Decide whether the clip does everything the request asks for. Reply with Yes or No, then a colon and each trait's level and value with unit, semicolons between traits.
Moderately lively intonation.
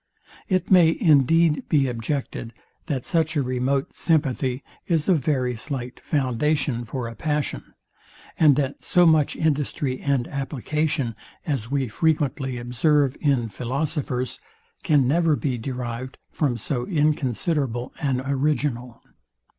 Yes: average, 3.4 semitones